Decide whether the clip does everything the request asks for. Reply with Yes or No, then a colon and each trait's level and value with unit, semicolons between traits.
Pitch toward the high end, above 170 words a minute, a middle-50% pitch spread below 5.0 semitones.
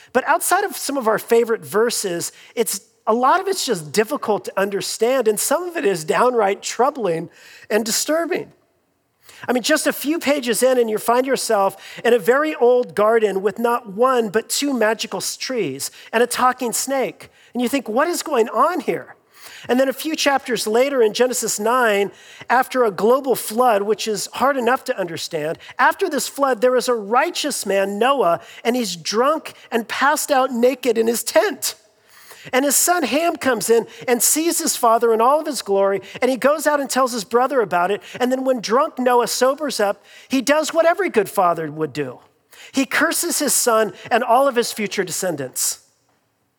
Yes: high, 245 Hz; average, 190 wpm; average, 4.2 semitones